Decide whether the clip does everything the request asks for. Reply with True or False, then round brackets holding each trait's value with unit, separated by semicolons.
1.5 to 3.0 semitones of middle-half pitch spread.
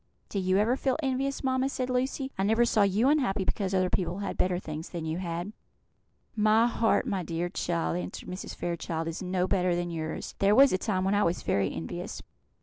False (4.7 semitones)